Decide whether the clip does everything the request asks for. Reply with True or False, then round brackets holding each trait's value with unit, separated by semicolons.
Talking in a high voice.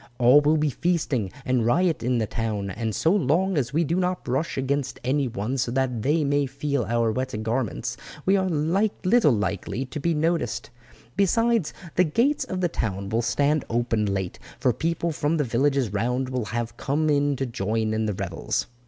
False (135 Hz)